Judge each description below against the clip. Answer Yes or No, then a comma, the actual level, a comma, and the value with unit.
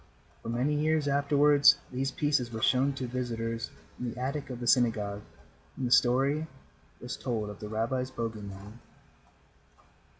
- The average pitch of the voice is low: Yes, low, 125 Hz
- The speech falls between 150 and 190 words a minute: Yes, average, 155 wpm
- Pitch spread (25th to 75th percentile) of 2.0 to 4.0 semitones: Yes, average, 3.5 semitones